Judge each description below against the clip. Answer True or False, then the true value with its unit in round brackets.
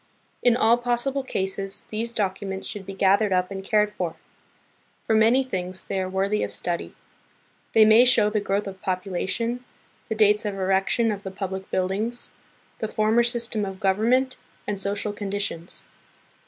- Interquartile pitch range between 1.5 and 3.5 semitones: True (2.8 semitones)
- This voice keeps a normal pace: True (160 wpm)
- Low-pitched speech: False (205 Hz)